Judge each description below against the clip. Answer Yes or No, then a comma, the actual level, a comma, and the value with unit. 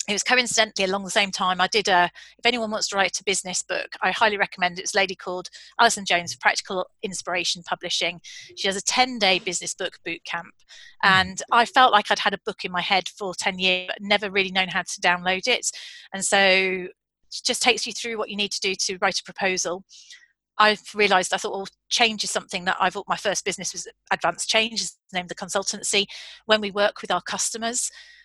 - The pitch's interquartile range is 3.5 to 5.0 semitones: No, average, 2.8 semitones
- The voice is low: No, high, 195 Hz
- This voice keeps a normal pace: No, fast, 225 wpm